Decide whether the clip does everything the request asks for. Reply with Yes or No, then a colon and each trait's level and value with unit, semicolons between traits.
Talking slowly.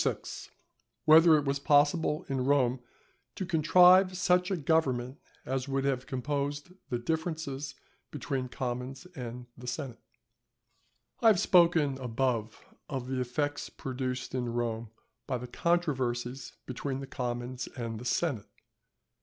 Yes: slow, 130 wpm